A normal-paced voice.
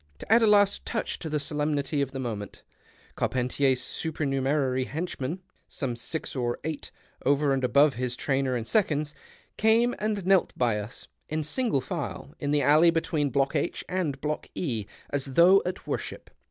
Yes: average, 165 wpm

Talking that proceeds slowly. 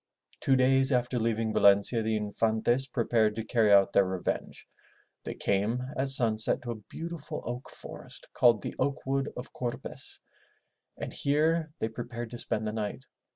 No: average, 160 wpm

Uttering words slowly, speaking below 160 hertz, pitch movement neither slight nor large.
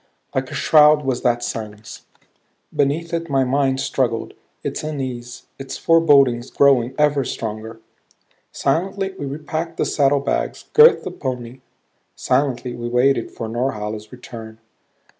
Yes: slow, 125 wpm; low, 135 Hz; average, 3.5 semitones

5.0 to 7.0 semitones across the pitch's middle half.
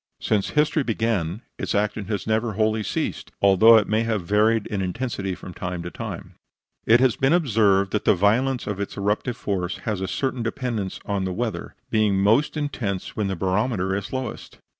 No: average, 3.1 semitones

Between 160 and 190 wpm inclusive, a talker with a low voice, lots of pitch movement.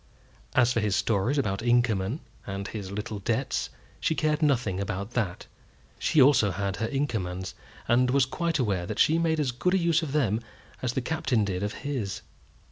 Yes: average, 180 wpm; low, 120 Hz; wide, 6.1 semitones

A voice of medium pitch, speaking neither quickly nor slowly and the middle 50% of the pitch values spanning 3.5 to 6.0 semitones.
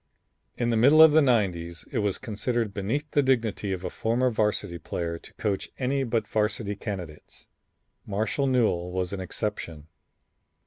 No: low, 105 Hz; average, 145 wpm; average, 4.9 semitones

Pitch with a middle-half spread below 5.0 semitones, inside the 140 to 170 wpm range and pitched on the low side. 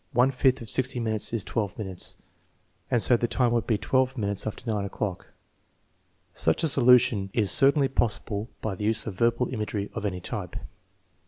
No: average, 3.4 semitones; average, 180 wpm; low, 115 Hz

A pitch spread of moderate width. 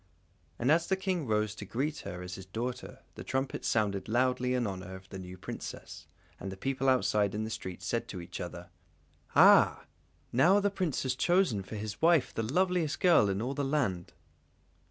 No: wide, 6.9 semitones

